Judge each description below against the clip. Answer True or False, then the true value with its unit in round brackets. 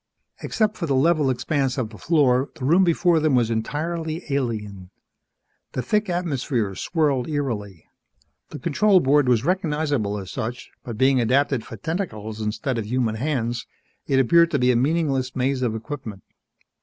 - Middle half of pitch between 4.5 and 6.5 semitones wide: True (5.3 semitones)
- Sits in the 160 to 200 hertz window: False (135 Hz)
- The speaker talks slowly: False (160 wpm)